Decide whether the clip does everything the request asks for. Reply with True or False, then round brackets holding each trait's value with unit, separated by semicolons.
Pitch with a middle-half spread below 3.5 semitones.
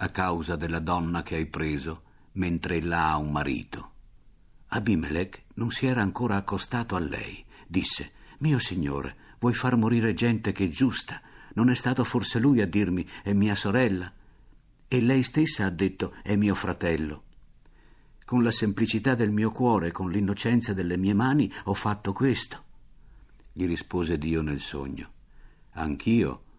False (5.5 semitones)